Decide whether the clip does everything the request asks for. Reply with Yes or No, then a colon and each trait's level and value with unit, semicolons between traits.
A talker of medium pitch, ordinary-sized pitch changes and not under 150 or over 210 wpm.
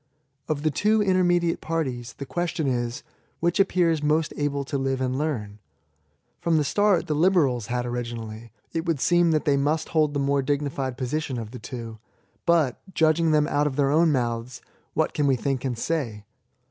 Yes: medium, 145 Hz; average, 4.4 semitones; average, 185 wpm